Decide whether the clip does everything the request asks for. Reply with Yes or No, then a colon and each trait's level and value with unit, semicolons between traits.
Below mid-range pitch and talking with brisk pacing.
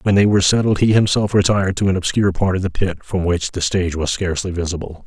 Yes: very low, 95 Hz; fast, 250 wpm